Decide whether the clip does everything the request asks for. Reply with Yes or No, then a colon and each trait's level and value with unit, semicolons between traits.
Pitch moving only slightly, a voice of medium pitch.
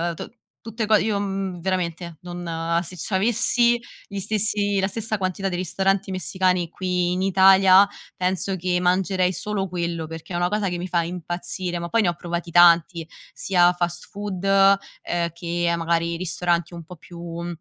Yes: narrow, 2.1 semitones; medium, 180 Hz